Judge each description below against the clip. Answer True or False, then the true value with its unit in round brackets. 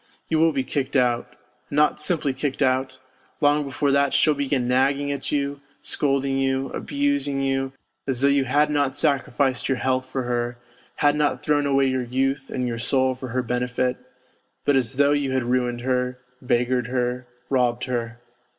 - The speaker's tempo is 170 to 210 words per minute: True (180 wpm)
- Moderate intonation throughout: False (2.1 semitones)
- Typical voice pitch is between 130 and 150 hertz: True (135 Hz)